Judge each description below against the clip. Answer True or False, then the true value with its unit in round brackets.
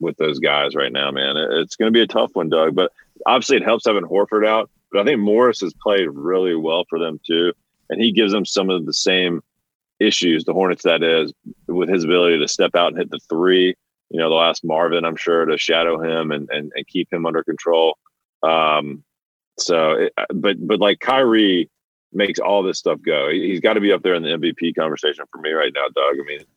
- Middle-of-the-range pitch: False (85 Hz)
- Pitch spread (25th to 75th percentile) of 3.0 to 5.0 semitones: False (2.6 semitones)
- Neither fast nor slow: False (230 wpm)